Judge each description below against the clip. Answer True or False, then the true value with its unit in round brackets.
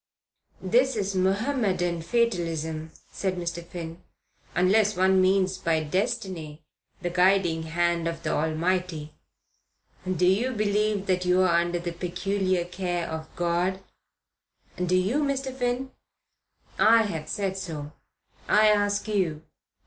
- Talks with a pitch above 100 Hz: True (185 Hz)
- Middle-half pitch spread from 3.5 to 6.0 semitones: False (3.1 semitones)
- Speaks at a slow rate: True (120 wpm)